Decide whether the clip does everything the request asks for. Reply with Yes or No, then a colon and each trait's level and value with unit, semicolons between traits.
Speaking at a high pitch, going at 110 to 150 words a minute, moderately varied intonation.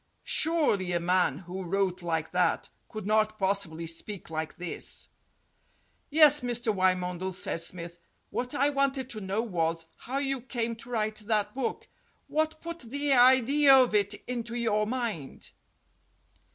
No: high, 215 Hz; average, 145 wpm; wide, 6.0 semitones